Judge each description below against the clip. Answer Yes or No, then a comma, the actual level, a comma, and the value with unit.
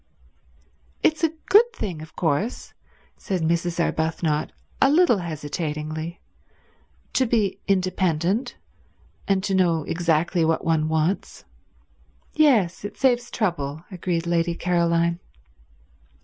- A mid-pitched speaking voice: Yes, medium, 170 Hz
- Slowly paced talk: Yes, slow, 105 wpm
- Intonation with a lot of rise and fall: No, average, 3.7 semitones